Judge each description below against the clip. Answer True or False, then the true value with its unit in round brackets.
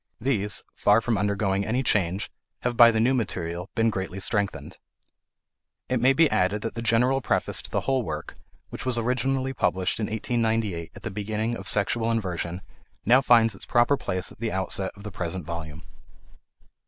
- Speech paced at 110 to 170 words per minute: False (180 wpm)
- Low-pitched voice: True (110 Hz)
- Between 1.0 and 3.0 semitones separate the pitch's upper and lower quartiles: False (3.8 semitones)